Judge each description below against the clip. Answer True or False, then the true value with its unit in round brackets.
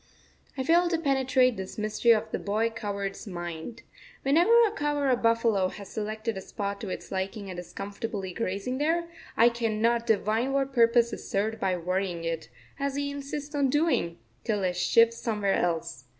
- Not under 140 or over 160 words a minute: False (180 wpm)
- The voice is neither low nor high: False (225 Hz)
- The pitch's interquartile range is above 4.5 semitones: True (5.2 semitones)